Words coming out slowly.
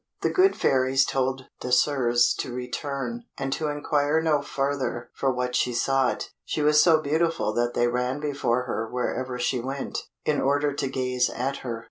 No: average, 170 wpm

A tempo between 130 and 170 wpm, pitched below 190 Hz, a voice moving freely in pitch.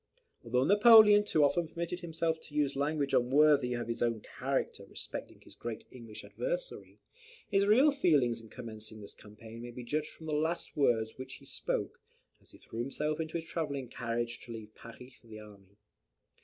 No: average, 185 wpm; low, 135 Hz; wide, 5.7 semitones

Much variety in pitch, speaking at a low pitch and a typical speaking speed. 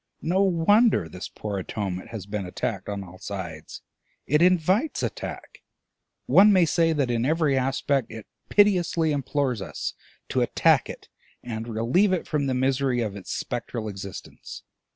Yes: wide, 8.1 semitones; low, 130 Hz; average, 150 wpm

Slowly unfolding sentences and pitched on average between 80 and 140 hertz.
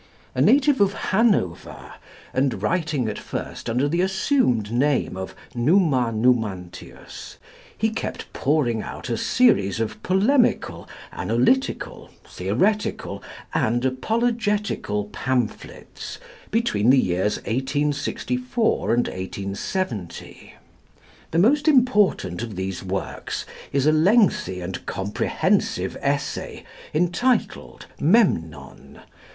Yes: slow, 100 wpm; low, 135 Hz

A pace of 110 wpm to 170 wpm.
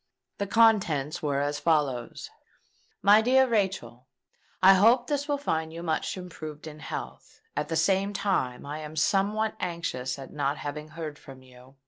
Yes: average, 160 wpm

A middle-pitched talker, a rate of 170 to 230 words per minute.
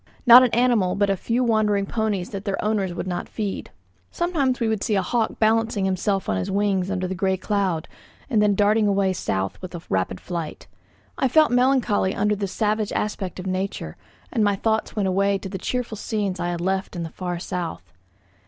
No: high, 200 Hz; average, 200 wpm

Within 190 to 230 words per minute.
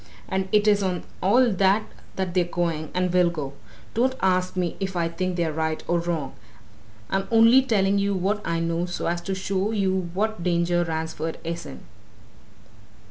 No: average, 180 wpm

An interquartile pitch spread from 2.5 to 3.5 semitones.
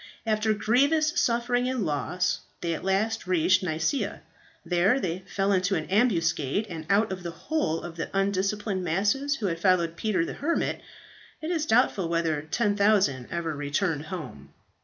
No: average, 4.9 semitones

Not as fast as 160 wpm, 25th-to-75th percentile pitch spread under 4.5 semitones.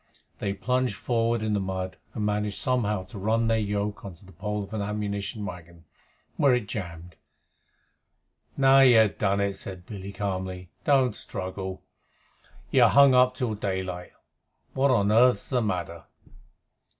Yes: average, 150 wpm; average, 3.3 semitones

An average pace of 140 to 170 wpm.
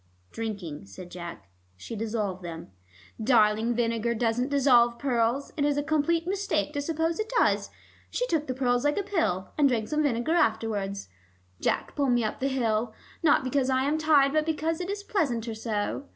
No: average, 185 wpm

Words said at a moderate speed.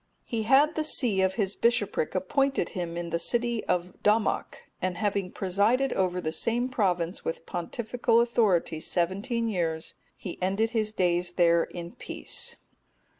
Yes: average, 145 wpm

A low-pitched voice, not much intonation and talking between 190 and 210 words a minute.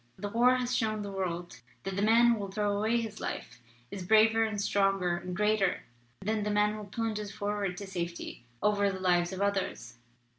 No: high, 205 Hz; narrow, 2.3 semitones; average, 195 wpm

